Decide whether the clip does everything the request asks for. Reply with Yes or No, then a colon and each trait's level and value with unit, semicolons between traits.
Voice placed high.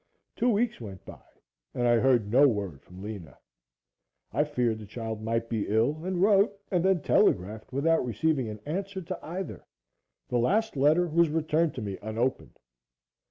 No: low, 130 Hz